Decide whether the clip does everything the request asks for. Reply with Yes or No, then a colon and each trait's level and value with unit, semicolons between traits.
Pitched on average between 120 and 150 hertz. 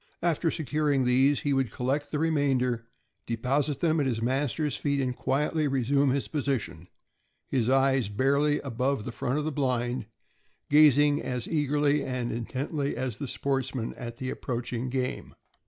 Yes: low, 135 Hz